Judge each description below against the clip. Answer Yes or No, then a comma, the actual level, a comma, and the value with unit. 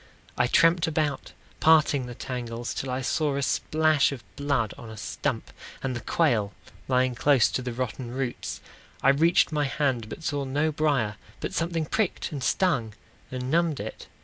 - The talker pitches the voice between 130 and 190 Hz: Yes, low, 135 Hz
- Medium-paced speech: Yes, average, 175 wpm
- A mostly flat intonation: No, average, 3.9 semitones